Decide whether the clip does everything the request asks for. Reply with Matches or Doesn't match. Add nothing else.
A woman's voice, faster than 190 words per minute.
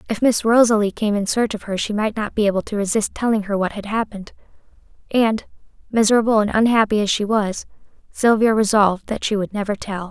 Matches